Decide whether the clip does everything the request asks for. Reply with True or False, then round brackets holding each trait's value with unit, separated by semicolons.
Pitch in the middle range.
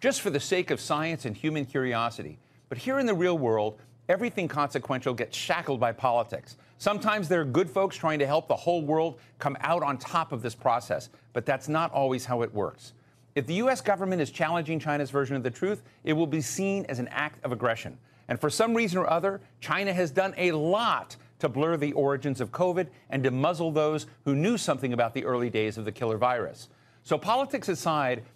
True (145 Hz)